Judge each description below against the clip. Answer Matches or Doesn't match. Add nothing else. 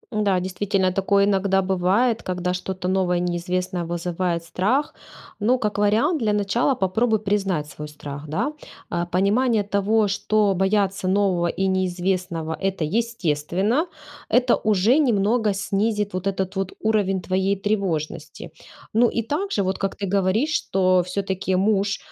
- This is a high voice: Matches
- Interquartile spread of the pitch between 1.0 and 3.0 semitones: Matches